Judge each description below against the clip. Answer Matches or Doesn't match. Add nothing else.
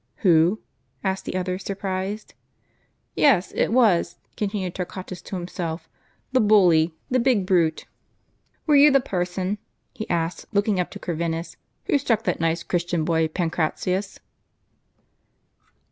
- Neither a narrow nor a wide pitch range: Matches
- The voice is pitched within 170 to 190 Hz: Matches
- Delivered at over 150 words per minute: Doesn't match